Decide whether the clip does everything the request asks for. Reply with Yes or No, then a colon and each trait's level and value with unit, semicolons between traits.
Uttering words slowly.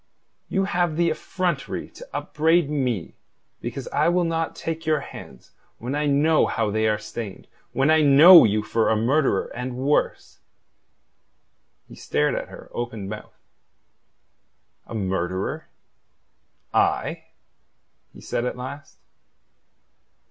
Yes: slow, 125 wpm